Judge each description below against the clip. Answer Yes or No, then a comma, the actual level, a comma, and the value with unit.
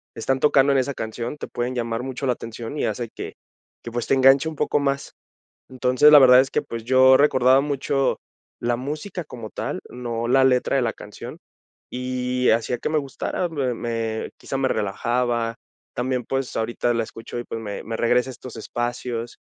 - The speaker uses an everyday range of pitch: No, narrow, 2.2 semitones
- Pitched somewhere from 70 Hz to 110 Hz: No, low, 125 Hz